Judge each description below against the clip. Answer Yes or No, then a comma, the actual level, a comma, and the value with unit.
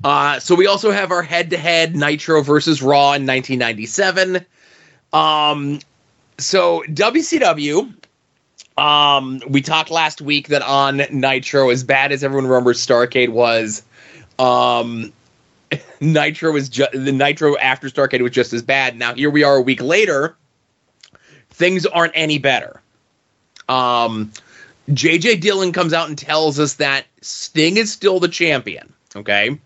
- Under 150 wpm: Yes, average, 140 wpm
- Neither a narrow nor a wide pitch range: Yes, average, 4.0 semitones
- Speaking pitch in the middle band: Yes, medium, 145 Hz